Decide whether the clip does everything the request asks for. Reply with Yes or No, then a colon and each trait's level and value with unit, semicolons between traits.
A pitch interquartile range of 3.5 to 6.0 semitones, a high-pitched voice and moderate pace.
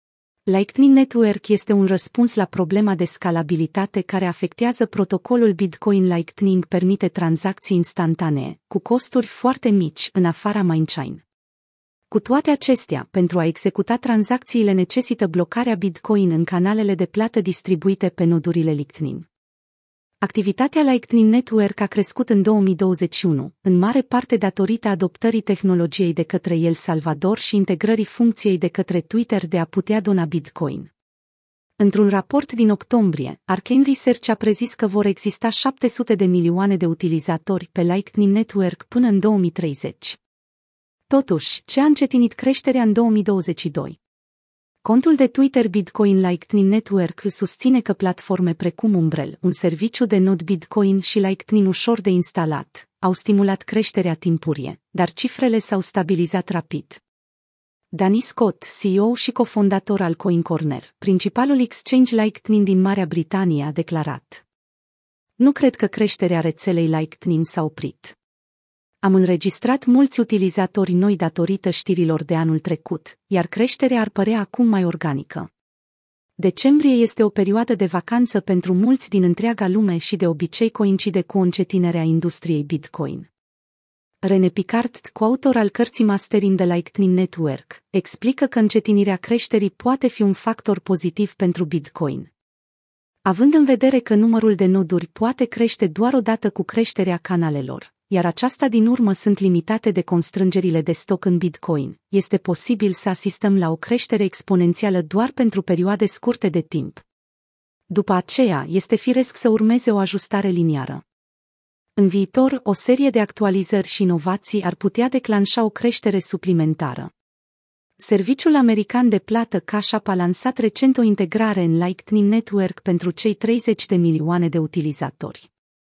Yes: average, 4.2 semitones; high, 195 Hz; average, 140 wpm